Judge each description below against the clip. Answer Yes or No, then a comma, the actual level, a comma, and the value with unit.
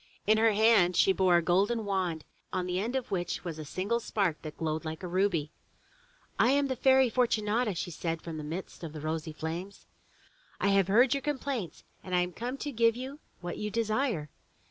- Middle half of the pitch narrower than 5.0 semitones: No, wide, 5.4 semitones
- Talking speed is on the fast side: Yes, fast, 210 wpm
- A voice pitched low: No, high, 195 Hz